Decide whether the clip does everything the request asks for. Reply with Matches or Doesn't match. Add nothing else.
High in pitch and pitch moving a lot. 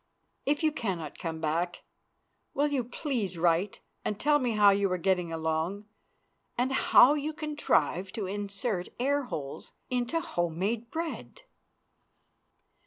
Matches